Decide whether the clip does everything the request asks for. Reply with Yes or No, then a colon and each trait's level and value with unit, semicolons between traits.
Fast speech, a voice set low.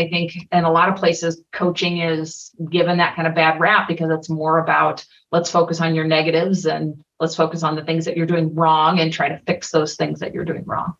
No: fast, 240 wpm; medium, 165 Hz